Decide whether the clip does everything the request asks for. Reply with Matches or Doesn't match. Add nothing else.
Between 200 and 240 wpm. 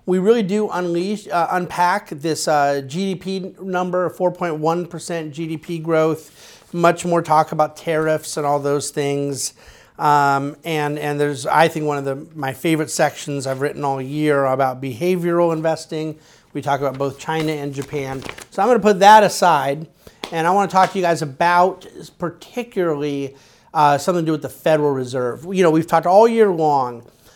Doesn't match